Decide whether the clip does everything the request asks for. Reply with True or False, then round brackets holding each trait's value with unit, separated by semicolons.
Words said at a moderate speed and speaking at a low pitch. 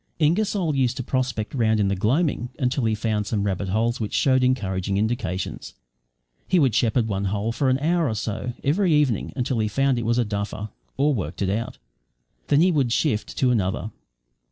True (195 wpm; 120 Hz)